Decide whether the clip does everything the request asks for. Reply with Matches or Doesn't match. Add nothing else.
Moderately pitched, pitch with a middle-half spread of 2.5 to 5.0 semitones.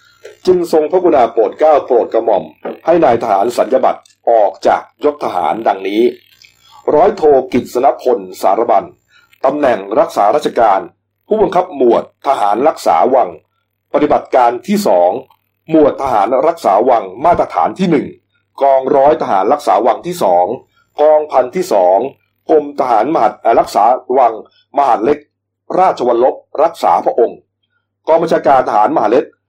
Doesn't match